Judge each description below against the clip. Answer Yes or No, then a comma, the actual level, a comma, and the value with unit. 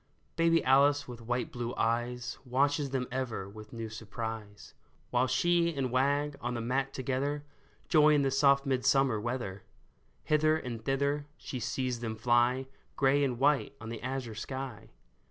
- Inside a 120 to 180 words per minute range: Yes, average, 155 wpm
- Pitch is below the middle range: Yes, low, 130 Hz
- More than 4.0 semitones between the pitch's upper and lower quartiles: No, average, 2.9 semitones